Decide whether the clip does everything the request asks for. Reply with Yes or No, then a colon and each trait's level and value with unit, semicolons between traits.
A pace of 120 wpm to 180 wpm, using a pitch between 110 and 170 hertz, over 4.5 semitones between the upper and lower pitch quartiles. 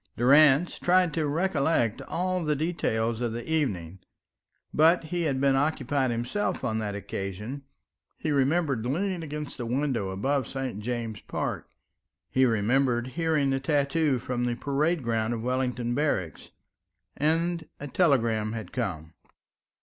Yes: average, 140 wpm; low, 135 Hz; average, 4.9 semitones